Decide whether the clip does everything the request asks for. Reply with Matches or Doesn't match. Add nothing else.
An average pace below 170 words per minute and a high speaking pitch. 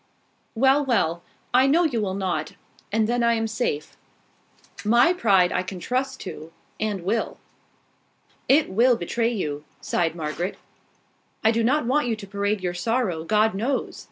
Matches